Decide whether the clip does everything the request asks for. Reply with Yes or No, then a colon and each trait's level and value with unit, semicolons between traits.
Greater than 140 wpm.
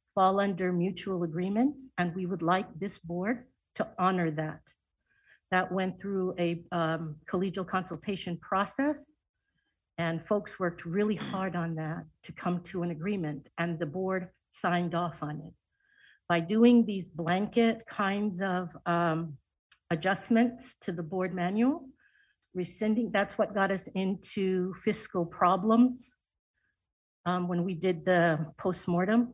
No: slow, 135 wpm